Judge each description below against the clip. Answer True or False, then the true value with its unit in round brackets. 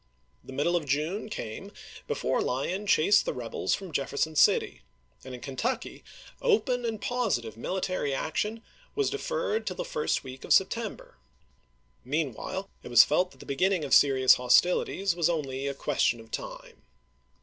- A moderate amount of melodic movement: False (7.6 semitones)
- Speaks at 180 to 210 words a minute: False (155 wpm)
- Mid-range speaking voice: True (160 Hz)